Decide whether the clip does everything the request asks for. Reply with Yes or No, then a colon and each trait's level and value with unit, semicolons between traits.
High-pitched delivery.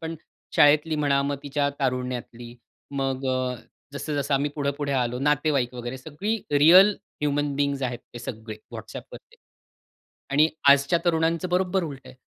No: medium, 140 Hz